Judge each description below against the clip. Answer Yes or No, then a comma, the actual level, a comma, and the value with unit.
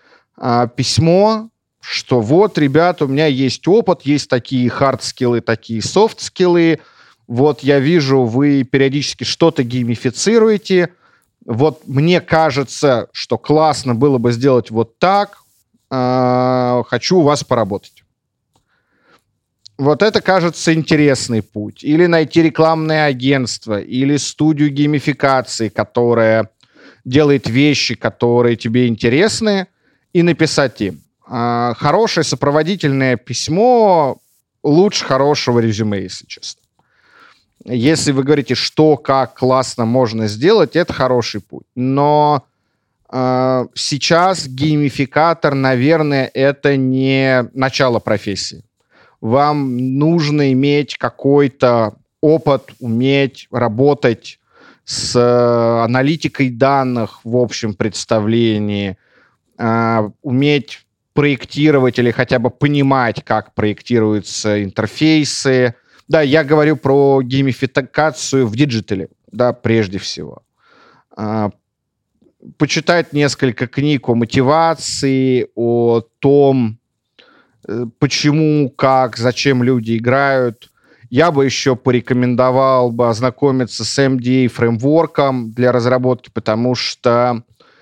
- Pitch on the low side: Yes, low, 130 Hz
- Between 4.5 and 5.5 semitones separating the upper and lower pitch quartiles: No, average, 3.7 semitones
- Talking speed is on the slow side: Yes, slow, 100 wpm